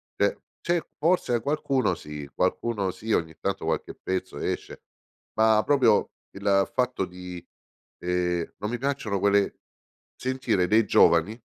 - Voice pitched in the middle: No, low, 100 Hz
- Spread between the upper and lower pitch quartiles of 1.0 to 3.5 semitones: No, average, 5.3 semitones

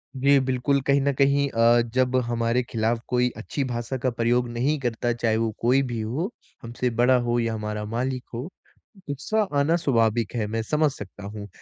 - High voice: No, low, 120 Hz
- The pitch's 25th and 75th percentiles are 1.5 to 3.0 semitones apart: Yes, narrow, 2.6 semitones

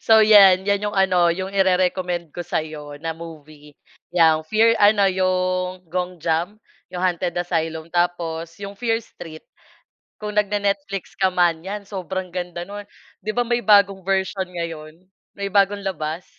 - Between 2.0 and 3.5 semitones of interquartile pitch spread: Yes, average, 2.9 semitones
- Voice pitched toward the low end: No, medium, 185 Hz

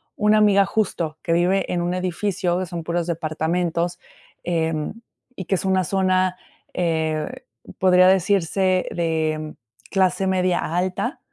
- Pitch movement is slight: Yes, narrow, 2.1 semitones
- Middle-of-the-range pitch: Yes, medium, 180 Hz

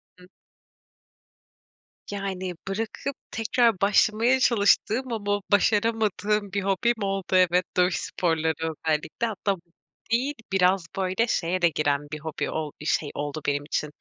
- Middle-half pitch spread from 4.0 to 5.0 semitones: Yes, average, 4.5 semitones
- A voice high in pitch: Yes, high, 195 Hz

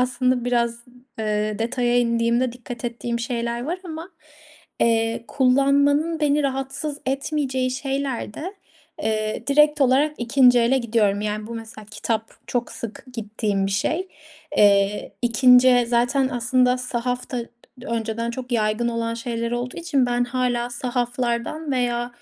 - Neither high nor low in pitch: No, high, 245 Hz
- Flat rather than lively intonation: Yes, narrow, 2.2 semitones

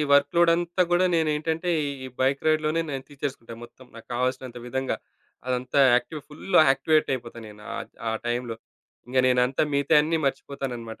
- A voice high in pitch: No, low, 135 Hz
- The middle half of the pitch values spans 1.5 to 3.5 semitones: No, average, 3.9 semitones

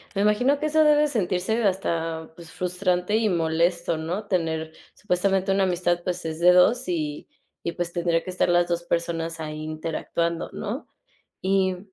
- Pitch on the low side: No, medium, 180 Hz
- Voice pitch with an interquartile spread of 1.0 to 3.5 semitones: Yes, average, 2.9 semitones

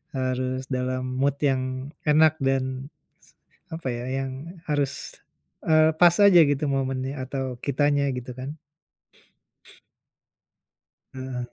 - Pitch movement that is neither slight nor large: No, narrow, 2.2 semitones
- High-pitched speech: No, low, 135 Hz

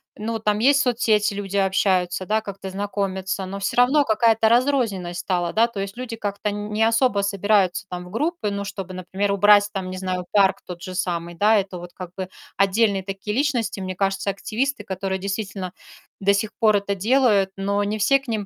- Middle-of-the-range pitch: No, high, 200 Hz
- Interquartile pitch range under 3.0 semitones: Yes, narrow, 2.5 semitones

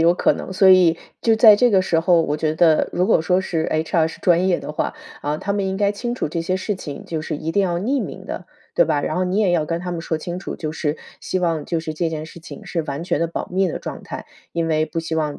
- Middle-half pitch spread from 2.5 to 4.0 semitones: Yes, average, 2.9 semitones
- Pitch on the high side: No, medium, 170 Hz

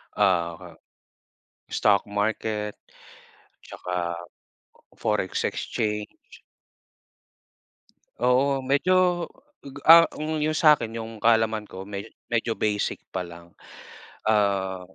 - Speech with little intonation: No, average, 4.5 semitones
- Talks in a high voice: No, low, 105 Hz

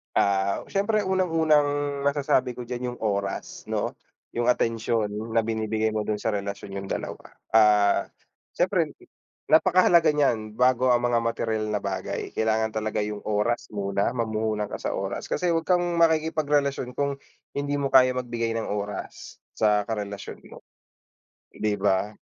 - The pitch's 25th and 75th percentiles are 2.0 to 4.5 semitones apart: No, average, 5.0 semitones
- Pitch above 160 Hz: No, low, 115 Hz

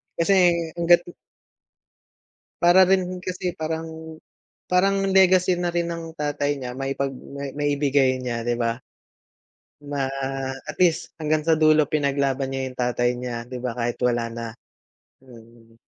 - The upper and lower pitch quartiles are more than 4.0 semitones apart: Yes, average, 5.0 semitones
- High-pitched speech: No, medium, 145 Hz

